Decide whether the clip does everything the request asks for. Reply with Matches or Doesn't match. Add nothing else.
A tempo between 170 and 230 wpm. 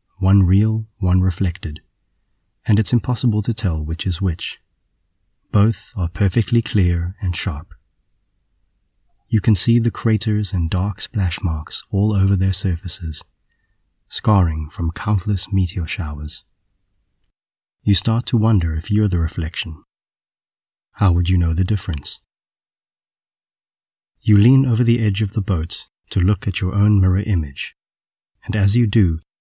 Doesn't match